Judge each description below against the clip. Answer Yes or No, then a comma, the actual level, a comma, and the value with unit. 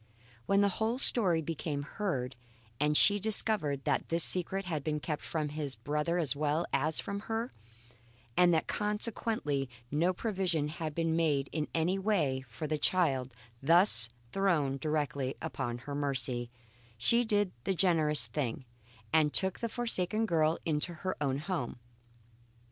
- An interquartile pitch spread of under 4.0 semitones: No, average, 4.9 semitones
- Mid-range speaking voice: Yes, medium, 160 Hz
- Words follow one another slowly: No, average, 150 wpm